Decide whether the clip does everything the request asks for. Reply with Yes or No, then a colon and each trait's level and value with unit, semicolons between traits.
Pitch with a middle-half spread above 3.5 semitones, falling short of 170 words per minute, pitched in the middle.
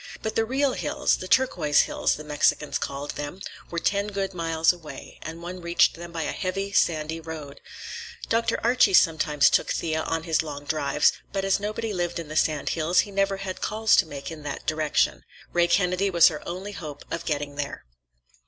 No: average, 4.1 semitones; average, 190 wpm; medium, 170 Hz